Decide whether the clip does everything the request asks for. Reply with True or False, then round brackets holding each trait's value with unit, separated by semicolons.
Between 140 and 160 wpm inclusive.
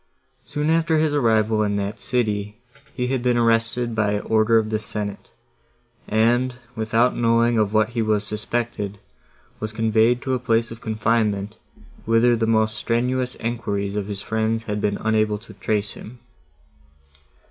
True (155 wpm)